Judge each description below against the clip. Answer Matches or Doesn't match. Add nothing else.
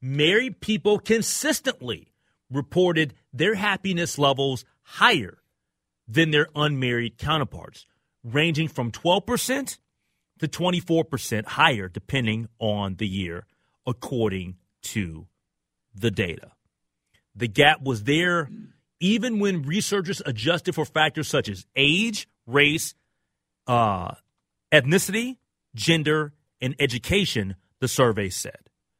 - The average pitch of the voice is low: Doesn't match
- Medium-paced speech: Doesn't match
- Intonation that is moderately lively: Doesn't match